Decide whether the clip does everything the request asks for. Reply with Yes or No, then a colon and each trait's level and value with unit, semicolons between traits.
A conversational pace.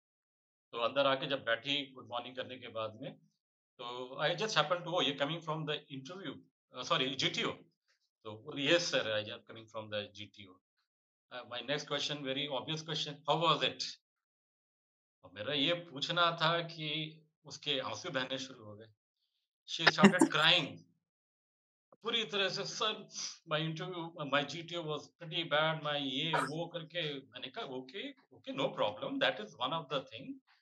Yes: average, 165 wpm